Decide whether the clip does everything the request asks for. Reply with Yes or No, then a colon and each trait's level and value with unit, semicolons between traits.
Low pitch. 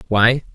Yes: low, 120 Hz